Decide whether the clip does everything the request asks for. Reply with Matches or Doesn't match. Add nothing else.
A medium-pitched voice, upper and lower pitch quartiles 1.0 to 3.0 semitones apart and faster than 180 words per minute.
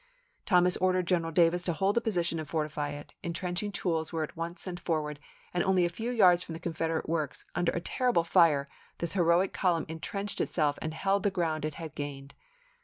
Matches